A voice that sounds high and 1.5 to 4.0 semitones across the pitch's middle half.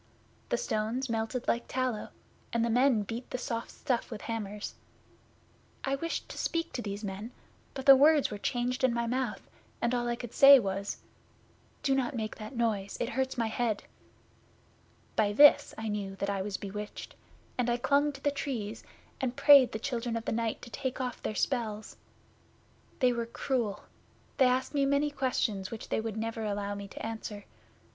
Yes: high, 235 Hz; average, 3.4 semitones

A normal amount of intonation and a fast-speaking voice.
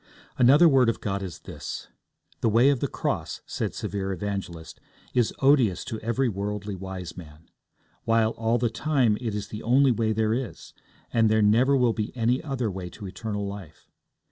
No: average, 3.6 semitones; average, 180 wpm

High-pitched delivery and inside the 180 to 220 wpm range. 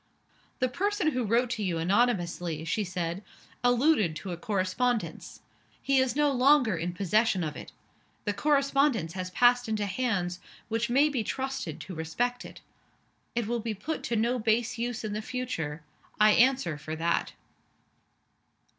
No: high, 225 Hz; average, 155 wpm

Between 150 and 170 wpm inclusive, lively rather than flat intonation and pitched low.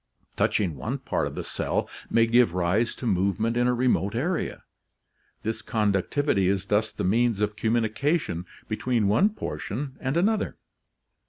No: average, 155 wpm; average, 3.8 semitones; low, 110 Hz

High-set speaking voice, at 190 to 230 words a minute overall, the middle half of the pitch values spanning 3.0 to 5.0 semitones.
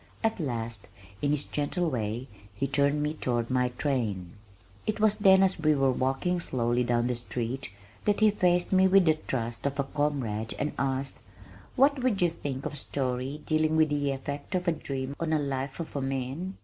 No: medium, 140 Hz; average, 200 wpm; average, 4.6 semitones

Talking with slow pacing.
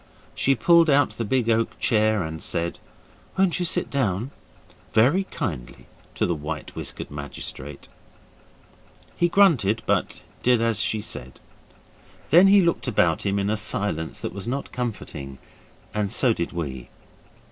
No: average, 145 wpm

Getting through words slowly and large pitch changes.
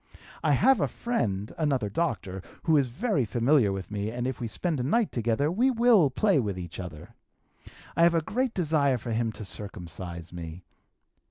No: average, 185 wpm; wide, 8.8 semitones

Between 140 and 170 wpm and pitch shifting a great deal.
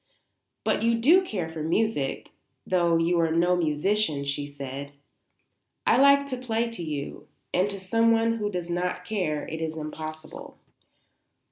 Yes: average, 150 wpm; wide, 6.1 semitones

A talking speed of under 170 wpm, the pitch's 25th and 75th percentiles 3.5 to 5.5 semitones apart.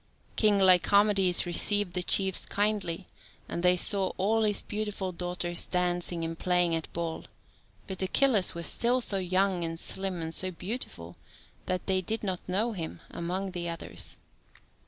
No: average, 155 wpm; narrow, 2.6 semitones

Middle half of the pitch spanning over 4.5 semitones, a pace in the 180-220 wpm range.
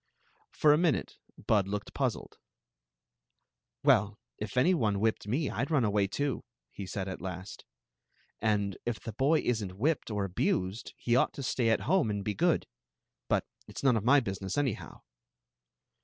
Yes: average, 5.2 semitones; average, 185 wpm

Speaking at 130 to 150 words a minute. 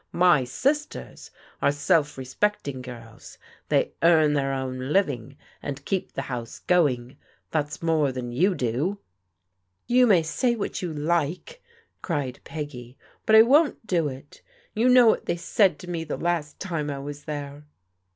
No: average, 160 wpm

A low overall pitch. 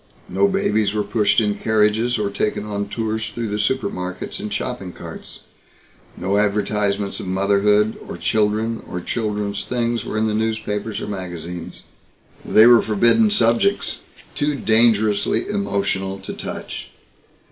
Yes: low, 105 Hz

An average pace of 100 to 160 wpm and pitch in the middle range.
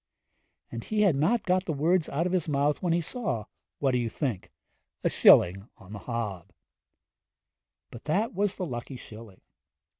No: average, 175 wpm; medium, 145 Hz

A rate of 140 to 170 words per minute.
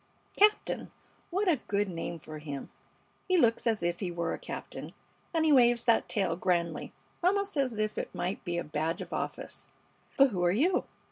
No: average, 190 wpm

